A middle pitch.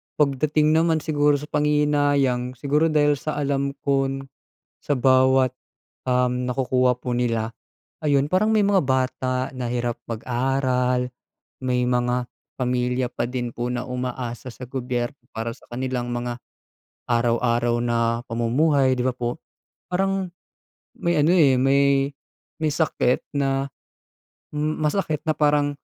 No: low, 130 Hz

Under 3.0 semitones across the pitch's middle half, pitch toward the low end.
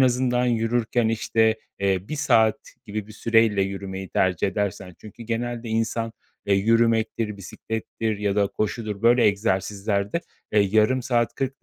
Yes: narrow, 2.6 semitones; low, 110 Hz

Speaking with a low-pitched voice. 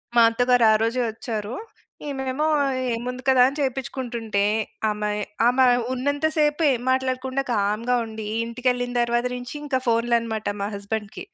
No: high, 245 Hz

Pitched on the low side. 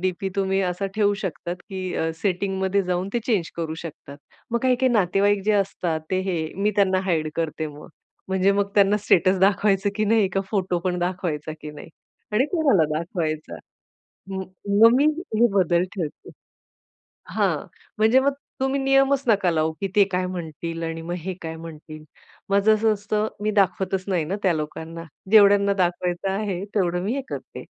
No: high, 190 Hz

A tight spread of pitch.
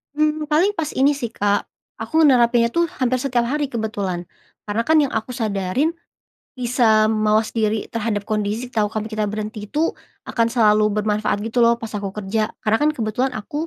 No: average, 3.2 semitones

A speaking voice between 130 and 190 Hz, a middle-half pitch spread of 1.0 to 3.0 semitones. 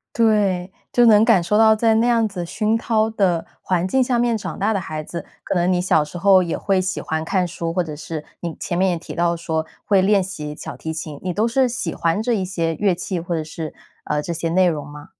No: medium, 185 Hz; average, 4.3 semitones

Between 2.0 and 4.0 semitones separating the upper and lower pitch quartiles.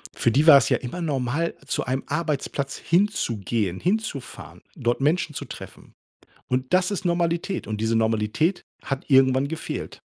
No: wide, 5.6 semitones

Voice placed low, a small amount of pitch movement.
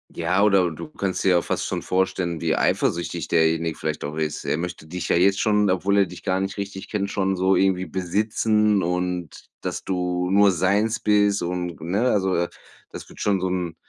Yes: very low, 95 Hz; narrow, 2.3 semitones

